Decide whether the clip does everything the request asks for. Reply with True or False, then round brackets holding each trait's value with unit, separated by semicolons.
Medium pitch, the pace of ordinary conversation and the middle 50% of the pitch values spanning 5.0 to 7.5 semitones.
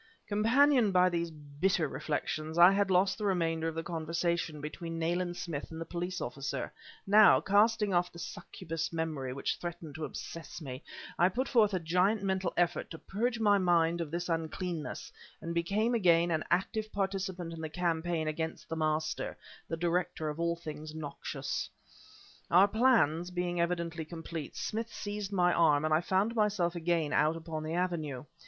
False (170 Hz; 170 wpm; 2.9 semitones)